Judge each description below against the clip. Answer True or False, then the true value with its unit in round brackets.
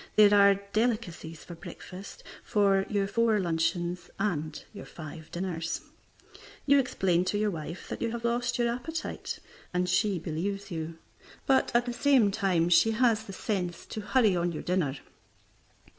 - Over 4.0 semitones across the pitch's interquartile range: True (4.5 semitones)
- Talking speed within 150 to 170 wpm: True (160 wpm)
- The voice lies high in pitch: True (195 Hz)